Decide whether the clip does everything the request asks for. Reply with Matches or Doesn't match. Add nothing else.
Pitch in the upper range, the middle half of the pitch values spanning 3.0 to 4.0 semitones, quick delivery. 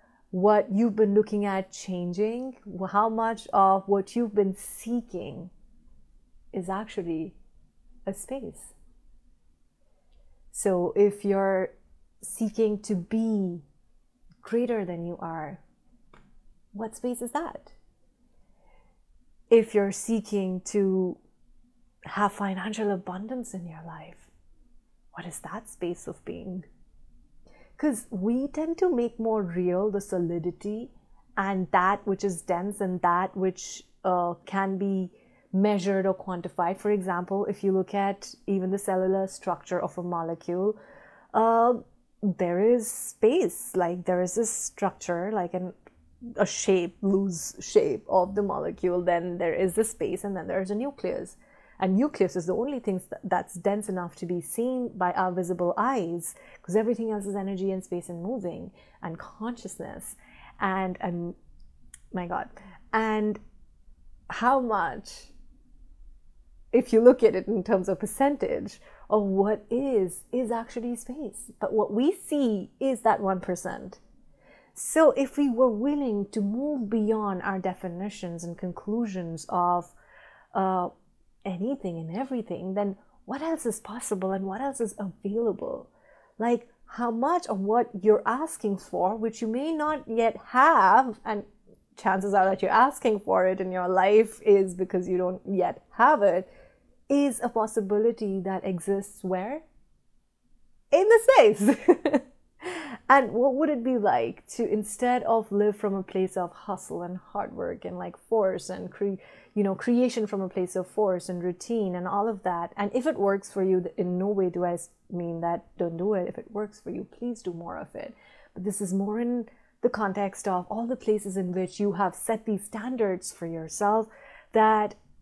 Doesn't match